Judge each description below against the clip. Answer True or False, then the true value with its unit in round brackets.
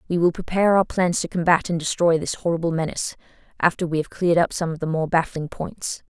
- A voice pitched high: False (170 Hz)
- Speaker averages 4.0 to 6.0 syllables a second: False (6.2 syllables/s)